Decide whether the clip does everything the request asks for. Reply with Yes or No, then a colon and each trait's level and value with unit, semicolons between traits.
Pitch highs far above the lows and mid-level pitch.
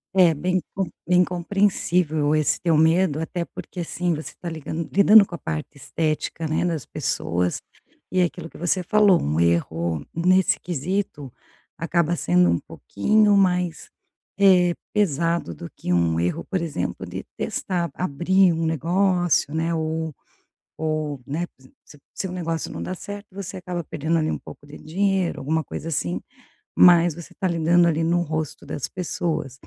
No: average, 3.2 semitones; medium, 165 Hz